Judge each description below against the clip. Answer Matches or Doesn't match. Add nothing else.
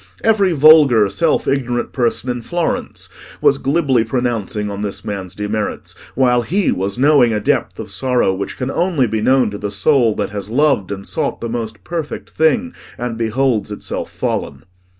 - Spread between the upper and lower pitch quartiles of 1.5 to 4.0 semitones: Doesn't match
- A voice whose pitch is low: Matches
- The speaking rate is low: Doesn't match